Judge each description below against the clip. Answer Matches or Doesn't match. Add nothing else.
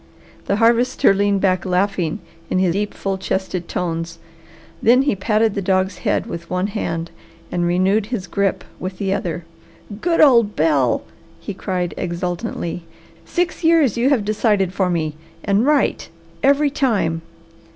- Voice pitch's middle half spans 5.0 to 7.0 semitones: Doesn't match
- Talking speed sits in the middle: Matches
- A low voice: Doesn't match